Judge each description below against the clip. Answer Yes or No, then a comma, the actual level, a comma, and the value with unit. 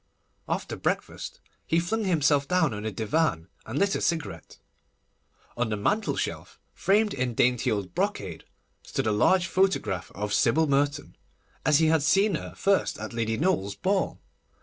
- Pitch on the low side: No, medium, 145 Hz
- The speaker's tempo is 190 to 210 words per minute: No, average, 160 wpm